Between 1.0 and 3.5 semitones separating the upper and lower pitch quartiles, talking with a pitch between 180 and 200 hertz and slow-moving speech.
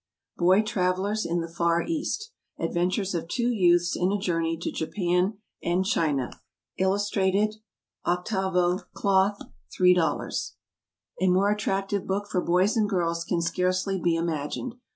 Yes: narrow, 2.6 semitones; medium, 185 Hz; slow, 130 wpm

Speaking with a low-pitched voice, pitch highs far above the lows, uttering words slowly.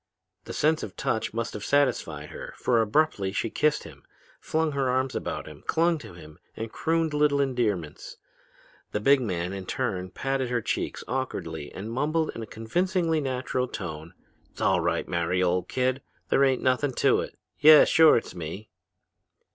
No: low, 125 Hz; wide, 7.4 semitones; average, 170 wpm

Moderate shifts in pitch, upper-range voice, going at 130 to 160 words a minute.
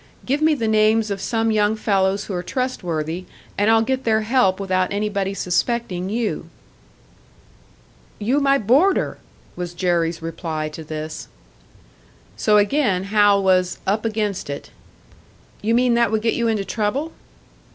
Yes: average, 3.8 semitones; high, 210 Hz; average, 145 wpm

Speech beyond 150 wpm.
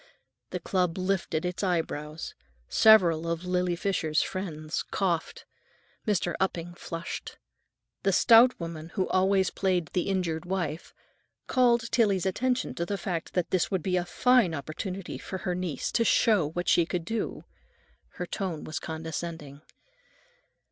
No: average, 140 wpm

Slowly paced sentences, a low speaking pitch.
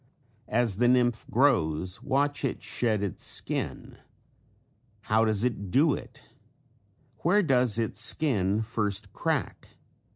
Yes: slow, 120 wpm; low, 115 Hz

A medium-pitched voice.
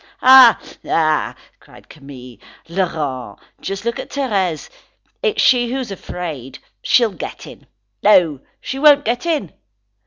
No: high, 195 Hz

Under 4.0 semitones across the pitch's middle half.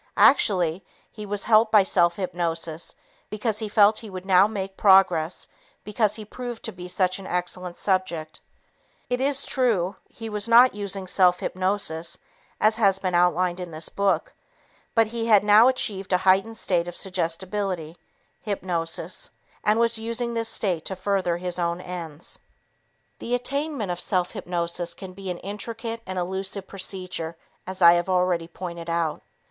Yes: average, 3.2 semitones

